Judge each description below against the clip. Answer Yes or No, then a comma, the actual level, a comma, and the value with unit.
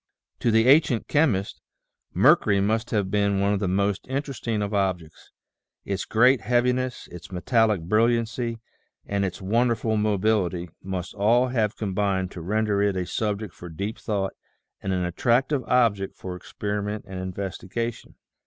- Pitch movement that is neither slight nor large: Yes, average, 3.3 semitones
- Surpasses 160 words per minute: No, average, 145 wpm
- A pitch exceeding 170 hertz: No, low, 105 Hz